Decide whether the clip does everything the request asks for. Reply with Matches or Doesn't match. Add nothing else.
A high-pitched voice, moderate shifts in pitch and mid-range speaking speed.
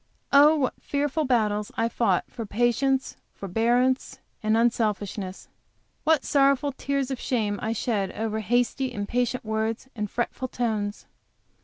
Doesn't match